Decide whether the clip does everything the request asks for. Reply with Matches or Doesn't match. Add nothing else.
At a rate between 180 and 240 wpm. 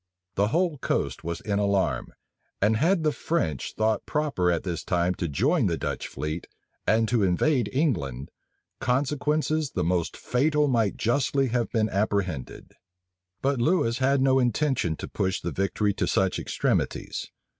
Doesn't match